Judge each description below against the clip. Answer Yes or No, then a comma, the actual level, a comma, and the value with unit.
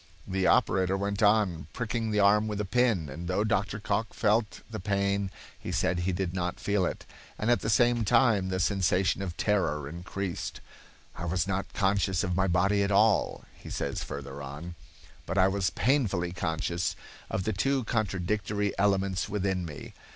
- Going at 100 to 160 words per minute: No, average, 175 wpm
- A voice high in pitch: No, very low, 95 Hz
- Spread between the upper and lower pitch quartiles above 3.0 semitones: No, narrow, 2.6 semitones